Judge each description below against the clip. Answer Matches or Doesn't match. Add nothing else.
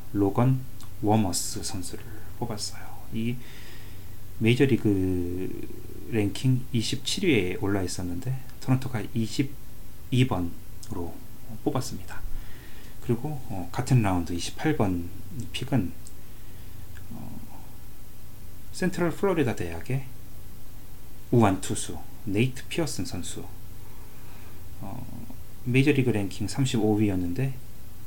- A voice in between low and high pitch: Doesn't match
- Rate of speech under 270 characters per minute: Matches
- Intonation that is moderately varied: Matches